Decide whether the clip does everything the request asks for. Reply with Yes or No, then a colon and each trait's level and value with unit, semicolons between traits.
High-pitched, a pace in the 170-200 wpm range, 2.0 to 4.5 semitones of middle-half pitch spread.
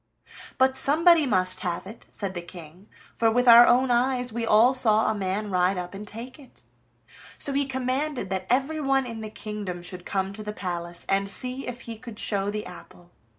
No: high, 215 Hz; average, 195 wpm; average, 5.1 semitones